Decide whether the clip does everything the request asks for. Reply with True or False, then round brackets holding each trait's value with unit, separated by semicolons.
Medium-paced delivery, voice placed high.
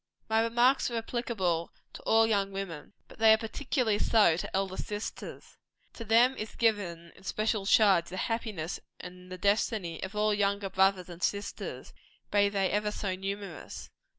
True (165 wpm; 205 Hz)